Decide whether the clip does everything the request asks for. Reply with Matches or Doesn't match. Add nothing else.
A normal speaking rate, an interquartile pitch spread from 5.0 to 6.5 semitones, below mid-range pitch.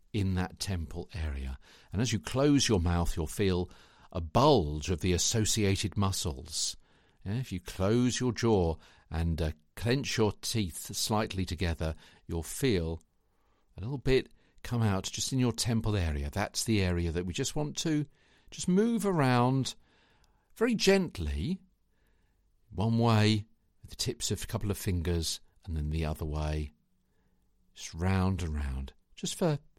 Matches